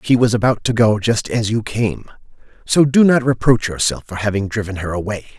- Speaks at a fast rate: Yes, fast, 210 wpm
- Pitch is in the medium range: No, low, 115 Hz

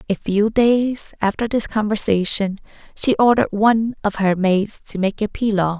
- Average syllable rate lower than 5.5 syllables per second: Yes, 4.7 syllables/s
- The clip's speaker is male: No, female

